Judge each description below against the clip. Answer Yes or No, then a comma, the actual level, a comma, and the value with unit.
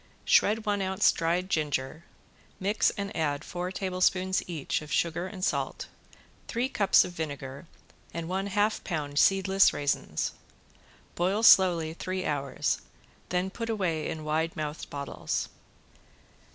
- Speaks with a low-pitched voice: No, medium, 180 Hz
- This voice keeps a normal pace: No, slow, 130 wpm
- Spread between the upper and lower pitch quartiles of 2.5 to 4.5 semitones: Yes, average, 3.8 semitones